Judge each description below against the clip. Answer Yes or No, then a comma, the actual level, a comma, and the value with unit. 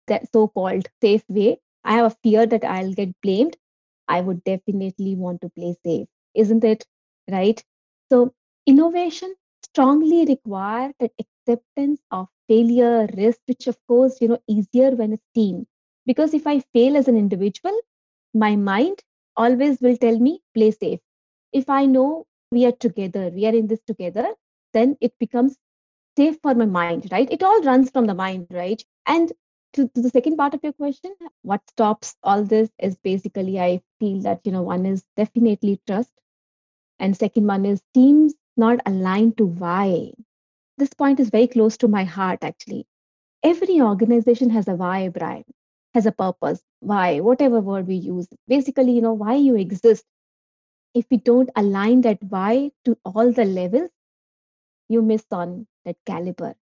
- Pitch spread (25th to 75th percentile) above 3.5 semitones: Yes, average, 4.6 semitones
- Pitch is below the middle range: No, high, 230 Hz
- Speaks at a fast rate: No, average, 165 wpm